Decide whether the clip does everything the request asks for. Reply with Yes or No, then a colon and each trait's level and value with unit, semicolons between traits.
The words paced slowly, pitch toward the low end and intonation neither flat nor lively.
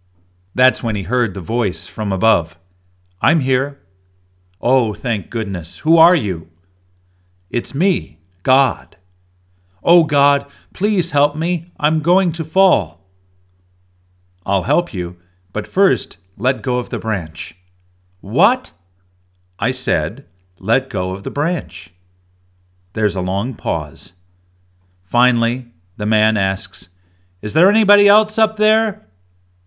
No: slow, 120 wpm; very low, 95 Hz; wide, 6.1 semitones